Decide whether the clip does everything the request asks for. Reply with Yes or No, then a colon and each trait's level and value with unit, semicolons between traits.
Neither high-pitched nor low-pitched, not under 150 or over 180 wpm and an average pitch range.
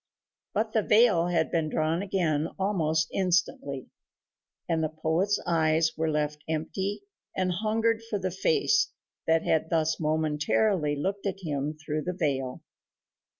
No: medium, 165 Hz; average, 140 wpm; average, 3.8 semitones